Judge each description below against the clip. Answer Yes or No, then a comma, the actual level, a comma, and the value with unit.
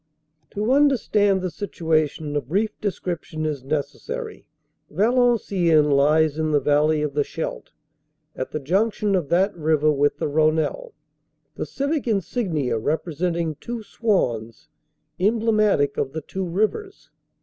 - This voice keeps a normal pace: No, slow, 130 wpm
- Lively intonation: Yes, wide, 6.0 semitones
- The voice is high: No, medium, 165 Hz